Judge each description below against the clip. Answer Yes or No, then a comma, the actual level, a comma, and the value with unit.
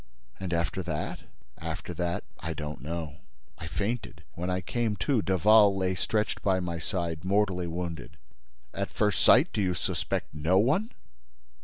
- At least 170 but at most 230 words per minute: No, average, 150 wpm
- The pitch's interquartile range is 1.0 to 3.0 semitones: No, average, 3.7 semitones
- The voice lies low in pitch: Yes, very low, 90 Hz